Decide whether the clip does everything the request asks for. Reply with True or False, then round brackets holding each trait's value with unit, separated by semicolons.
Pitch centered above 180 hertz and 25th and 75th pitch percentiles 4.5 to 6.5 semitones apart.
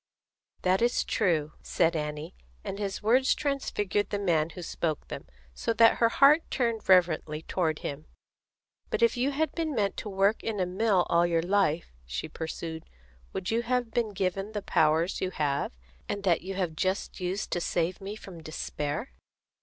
True (190 Hz; 5.0 semitones)